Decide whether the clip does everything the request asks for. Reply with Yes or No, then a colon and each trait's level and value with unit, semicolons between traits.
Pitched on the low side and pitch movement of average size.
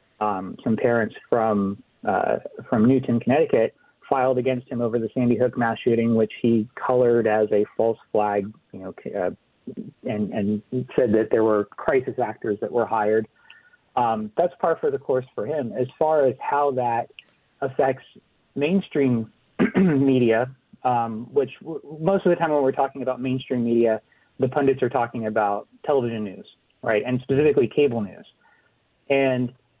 Yes: low, 125 Hz; average, 3.4 semitones